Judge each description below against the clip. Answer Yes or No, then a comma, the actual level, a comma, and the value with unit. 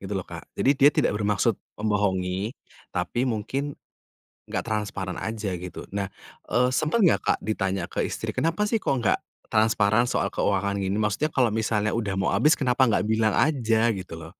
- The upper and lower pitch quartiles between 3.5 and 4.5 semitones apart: Yes, average, 4.0 semitones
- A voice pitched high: No, low, 110 Hz